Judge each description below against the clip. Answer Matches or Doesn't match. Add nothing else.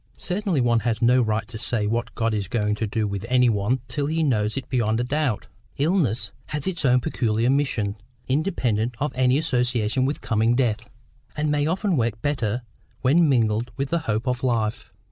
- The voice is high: Doesn't match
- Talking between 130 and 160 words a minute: Doesn't match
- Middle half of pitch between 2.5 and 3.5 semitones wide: Doesn't match